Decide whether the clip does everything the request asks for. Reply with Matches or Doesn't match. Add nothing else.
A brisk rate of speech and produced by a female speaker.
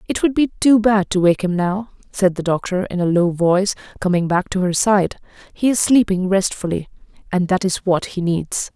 Matches